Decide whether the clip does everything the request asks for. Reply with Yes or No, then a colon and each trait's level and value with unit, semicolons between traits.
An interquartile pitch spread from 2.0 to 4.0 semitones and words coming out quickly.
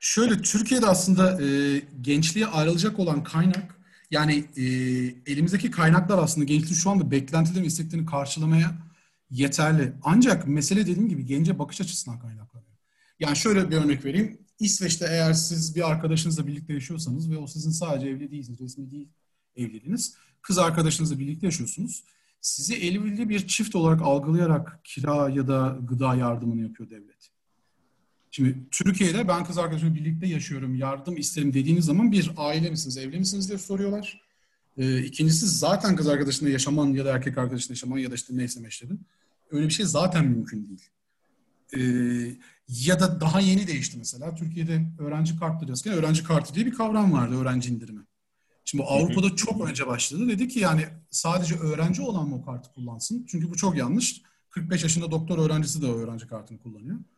No: average, 5.0 semitones; fast, 160 wpm